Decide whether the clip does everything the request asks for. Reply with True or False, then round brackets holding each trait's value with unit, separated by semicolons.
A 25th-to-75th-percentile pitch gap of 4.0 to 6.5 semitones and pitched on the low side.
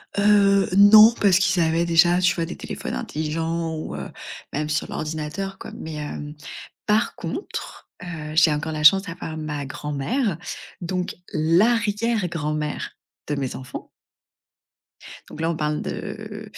False (4.5 semitones; 165 Hz)